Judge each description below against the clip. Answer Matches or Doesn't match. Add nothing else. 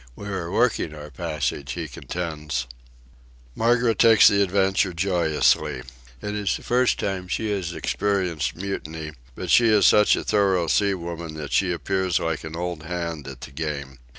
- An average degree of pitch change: Matches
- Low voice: Matches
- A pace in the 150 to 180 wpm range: Matches